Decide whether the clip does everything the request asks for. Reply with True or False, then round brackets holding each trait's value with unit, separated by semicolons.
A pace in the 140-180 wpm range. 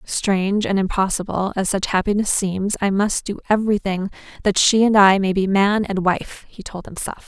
False (190 wpm)